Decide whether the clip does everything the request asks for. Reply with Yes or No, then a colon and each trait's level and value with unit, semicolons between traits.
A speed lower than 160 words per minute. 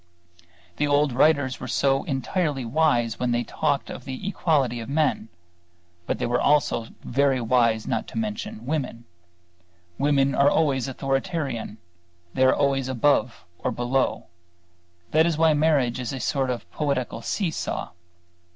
Yes: average, 145 wpm